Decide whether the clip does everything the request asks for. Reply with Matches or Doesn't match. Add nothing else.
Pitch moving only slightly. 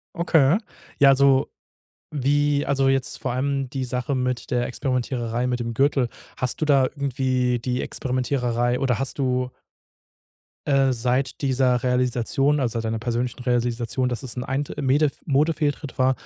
Matches